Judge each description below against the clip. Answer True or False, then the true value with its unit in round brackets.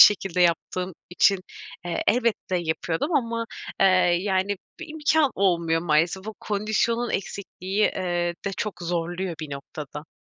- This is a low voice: False (185 Hz)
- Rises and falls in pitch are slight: False (3.7 semitones)